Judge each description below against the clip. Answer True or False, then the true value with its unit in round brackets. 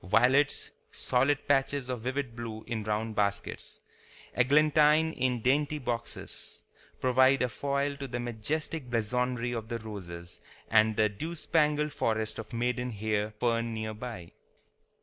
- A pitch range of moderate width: True (4.0 semitones)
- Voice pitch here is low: True (120 Hz)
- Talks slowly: True (130 wpm)